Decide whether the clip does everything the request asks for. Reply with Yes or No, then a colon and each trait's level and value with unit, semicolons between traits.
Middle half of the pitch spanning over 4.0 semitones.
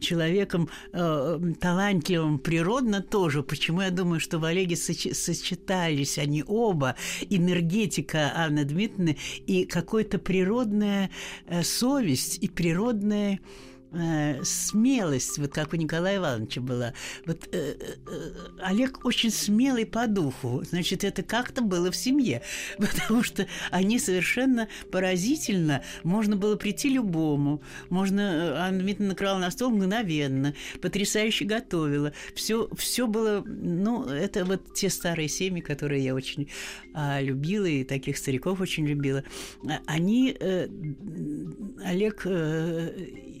Yes: average, 4.7 semitones